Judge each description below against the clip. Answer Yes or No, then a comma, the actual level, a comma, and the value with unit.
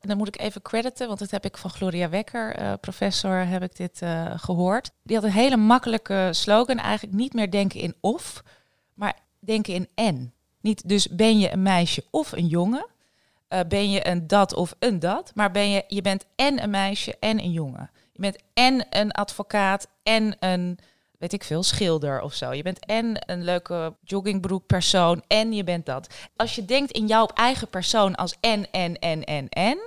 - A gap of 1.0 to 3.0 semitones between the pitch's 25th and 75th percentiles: No, average, 3.5 semitones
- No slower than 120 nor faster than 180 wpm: No, fast, 200 wpm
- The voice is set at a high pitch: Yes, high, 195 Hz